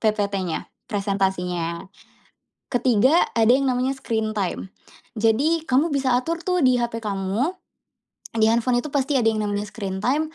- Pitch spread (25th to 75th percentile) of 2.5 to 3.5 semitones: No, average, 4.6 semitones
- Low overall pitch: No, high, 230 Hz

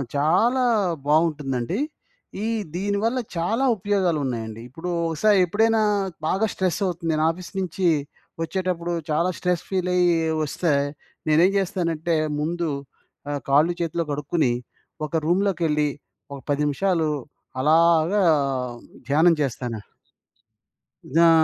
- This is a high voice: No, medium, 170 Hz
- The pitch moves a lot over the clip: No, average, 3.4 semitones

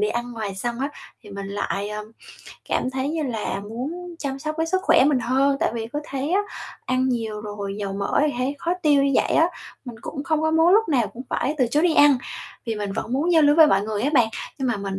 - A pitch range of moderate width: No, wide, 5.7 semitones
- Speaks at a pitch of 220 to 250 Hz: No, very high, 260 Hz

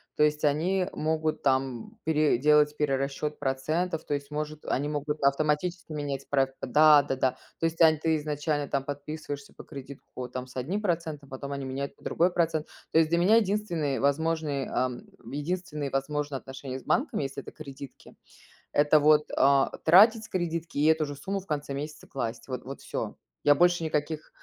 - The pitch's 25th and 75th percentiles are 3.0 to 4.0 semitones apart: No, narrow, 2.6 semitones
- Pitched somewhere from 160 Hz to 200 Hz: No, medium, 150 Hz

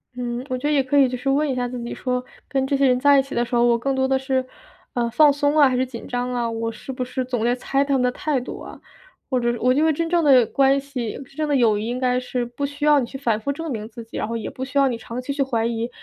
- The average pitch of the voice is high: Yes, very high, 255 Hz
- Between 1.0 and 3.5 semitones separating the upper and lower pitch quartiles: Yes, narrow, 2.5 semitones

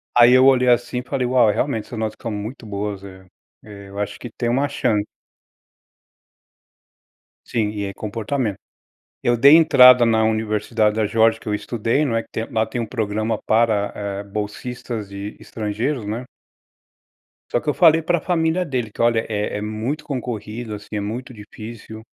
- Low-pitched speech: Yes, low, 110 Hz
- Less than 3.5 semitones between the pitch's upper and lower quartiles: Yes, average, 3.0 semitones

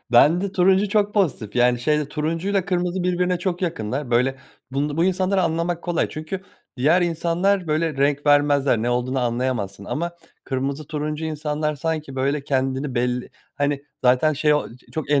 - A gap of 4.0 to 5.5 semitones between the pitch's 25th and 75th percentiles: Yes, average, 4.6 semitones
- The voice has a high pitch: No, medium, 150 Hz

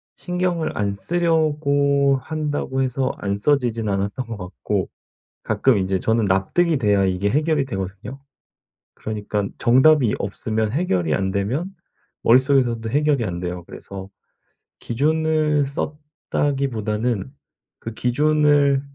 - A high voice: No, low, 130 Hz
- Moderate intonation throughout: No, wide, 6.4 semitones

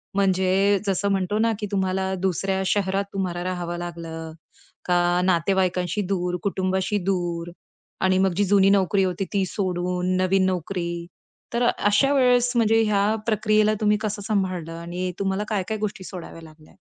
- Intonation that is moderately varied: No, narrow, 2.2 semitones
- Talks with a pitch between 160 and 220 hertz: Yes, high, 190 Hz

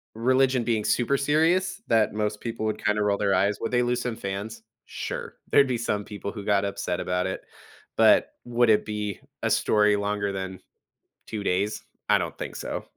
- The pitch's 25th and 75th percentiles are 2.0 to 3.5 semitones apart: Yes, average, 3.0 semitones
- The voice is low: Yes, low, 105 Hz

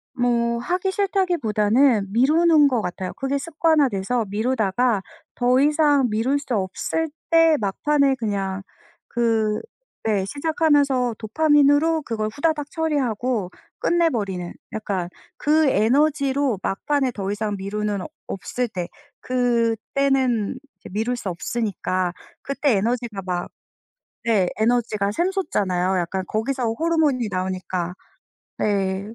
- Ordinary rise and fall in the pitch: No, wide, 5.9 semitones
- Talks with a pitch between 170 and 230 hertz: No, high, 240 Hz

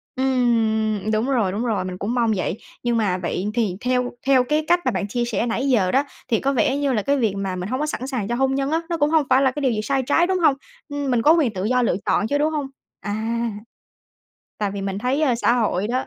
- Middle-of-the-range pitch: No, high, 245 Hz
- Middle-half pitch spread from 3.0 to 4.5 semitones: Yes, average, 4.2 semitones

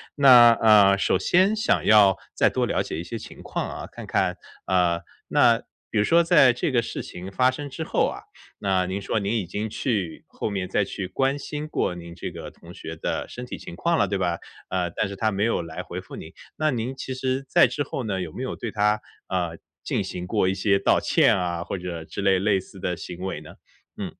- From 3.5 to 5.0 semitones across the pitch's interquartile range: No, wide, 5.4 semitones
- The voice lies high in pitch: No, low, 100 Hz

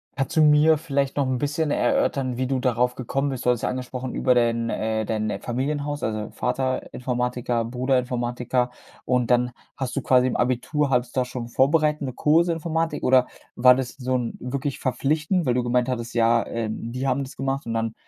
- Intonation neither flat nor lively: No, narrow, 2.2 semitones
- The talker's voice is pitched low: Yes, low, 125 Hz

